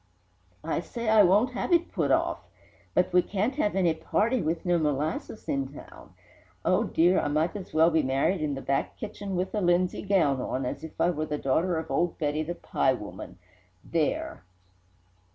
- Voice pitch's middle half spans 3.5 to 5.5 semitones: Yes, average, 4.6 semitones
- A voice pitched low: No, medium, 170 Hz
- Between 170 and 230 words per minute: Yes, average, 190 wpm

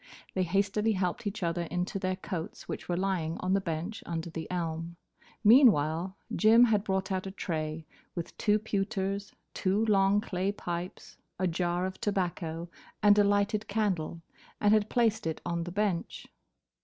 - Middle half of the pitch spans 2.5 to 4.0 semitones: Yes, average, 3.2 semitones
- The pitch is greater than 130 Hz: Yes, high, 190 Hz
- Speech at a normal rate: Yes, average, 165 wpm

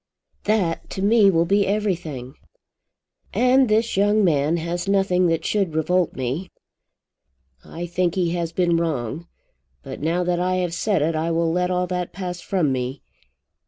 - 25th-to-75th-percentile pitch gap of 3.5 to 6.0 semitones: No, average, 2.8 semitones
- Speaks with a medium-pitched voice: Yes, medium, 175 Hz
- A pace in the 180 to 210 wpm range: No, average, 160 wpm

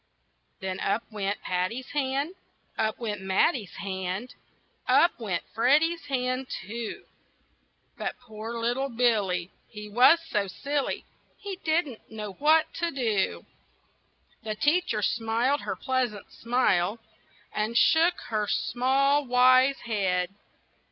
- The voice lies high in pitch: Yes, high, 235 Hz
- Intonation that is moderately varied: Yes, average, 4.8 semitones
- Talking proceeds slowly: Yes, slow, 115 wpm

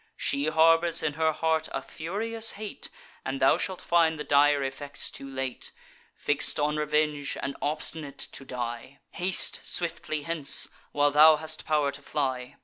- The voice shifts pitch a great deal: No, narrow, 2.5 semitones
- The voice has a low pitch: No, medium, 150 Hz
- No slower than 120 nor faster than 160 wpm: Yes, average, 155 wpm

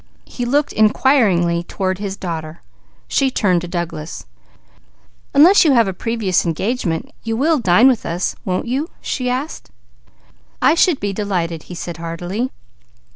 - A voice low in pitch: No, high, 200 Hz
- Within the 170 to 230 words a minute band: No, average, 145 wpm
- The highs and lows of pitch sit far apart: Yes, wide, 6.6 semitones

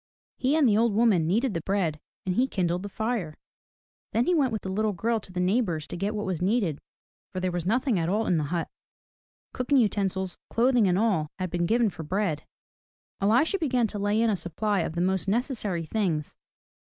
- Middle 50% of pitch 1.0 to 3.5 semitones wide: No, average, 4.5 semitones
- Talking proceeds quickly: Yes, fast, 215 wpm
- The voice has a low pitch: No, high, 200 Hz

